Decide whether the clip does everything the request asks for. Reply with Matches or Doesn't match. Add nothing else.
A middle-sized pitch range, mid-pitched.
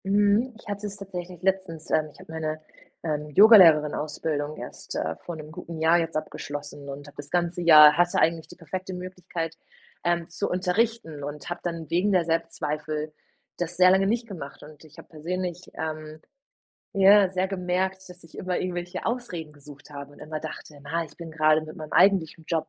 Matches